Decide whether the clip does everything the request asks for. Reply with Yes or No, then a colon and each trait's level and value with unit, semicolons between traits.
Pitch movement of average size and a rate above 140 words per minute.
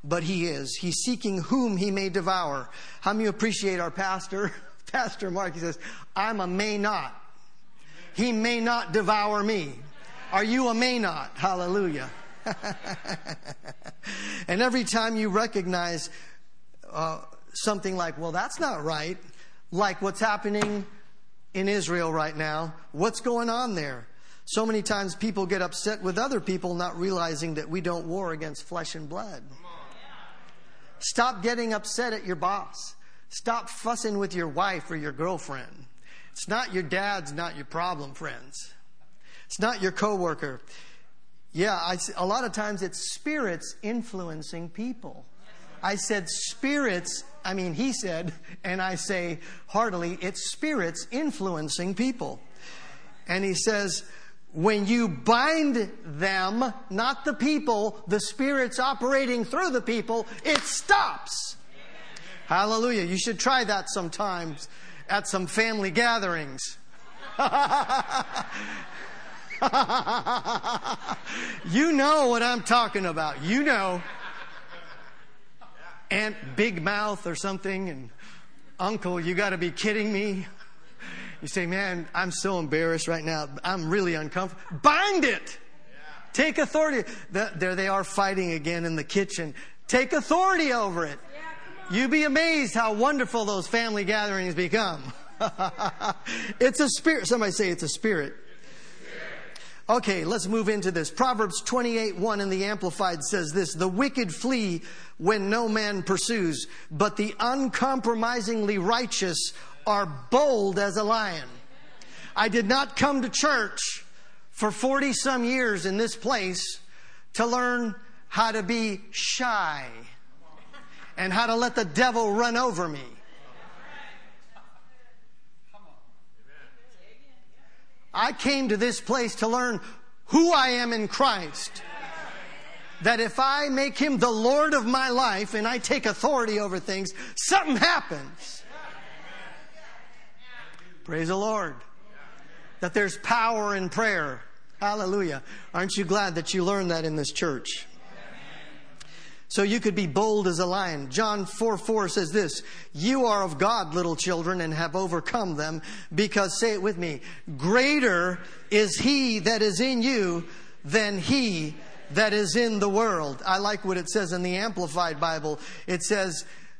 No: average, 4.6 semitones; slow, 135 wpm